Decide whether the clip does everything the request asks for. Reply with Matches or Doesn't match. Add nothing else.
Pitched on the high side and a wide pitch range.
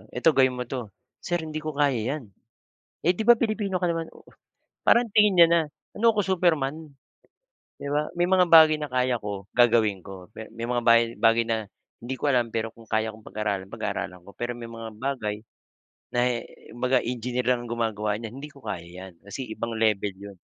Doesn't match